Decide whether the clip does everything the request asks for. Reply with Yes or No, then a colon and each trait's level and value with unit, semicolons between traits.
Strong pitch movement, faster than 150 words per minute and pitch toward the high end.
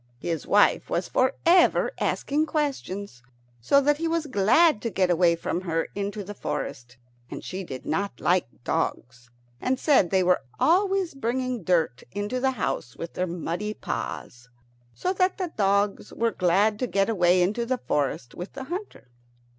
Yes: wide, 7.1 semitones; average, 170 wpm; high, 205 Hz